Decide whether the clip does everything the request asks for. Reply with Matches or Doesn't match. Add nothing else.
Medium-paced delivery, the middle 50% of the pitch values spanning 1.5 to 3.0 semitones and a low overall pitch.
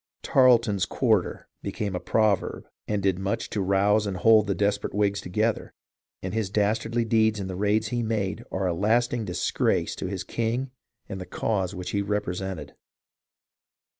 Matches